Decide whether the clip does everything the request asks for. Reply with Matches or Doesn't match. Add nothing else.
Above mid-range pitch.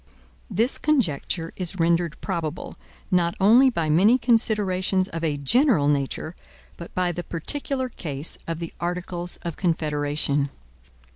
Doesn't match